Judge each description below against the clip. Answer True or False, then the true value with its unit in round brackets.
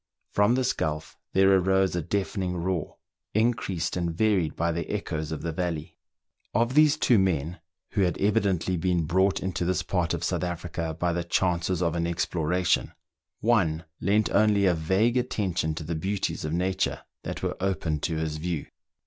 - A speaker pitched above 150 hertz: False (90 Hz)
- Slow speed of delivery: False (175 wpm)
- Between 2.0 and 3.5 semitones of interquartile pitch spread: True (3.0 semitones)